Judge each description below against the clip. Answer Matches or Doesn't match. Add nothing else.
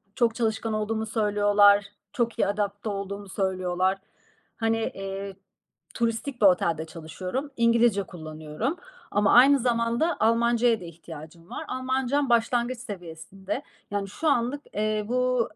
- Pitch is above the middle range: Matches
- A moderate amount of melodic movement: Matches